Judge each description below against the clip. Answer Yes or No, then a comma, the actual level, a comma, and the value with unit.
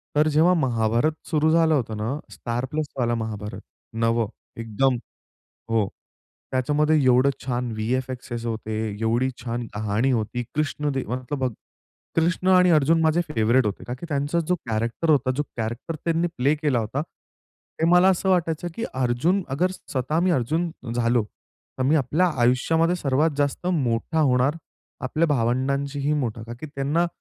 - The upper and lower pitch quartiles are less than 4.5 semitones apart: No, average, 4.9 semitones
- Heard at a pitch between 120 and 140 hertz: Yes, low, 135 Hz